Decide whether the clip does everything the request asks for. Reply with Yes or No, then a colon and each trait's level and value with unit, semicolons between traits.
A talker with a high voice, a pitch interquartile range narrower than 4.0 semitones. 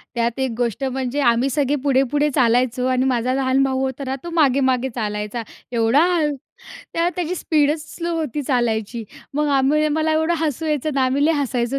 Yes: very high, 265 Hz; average, 3.3 semitones